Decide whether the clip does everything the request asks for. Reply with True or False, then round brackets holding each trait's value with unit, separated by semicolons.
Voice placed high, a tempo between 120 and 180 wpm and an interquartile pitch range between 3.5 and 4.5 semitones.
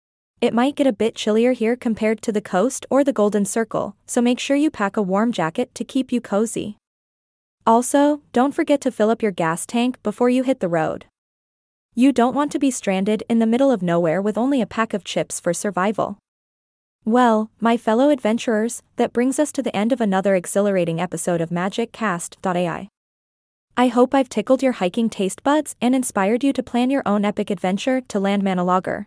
False (225 Hz; 200 wpm; 4.2 semitones)